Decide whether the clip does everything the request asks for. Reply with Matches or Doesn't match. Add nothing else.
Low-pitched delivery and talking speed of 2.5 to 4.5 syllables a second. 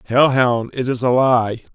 Matches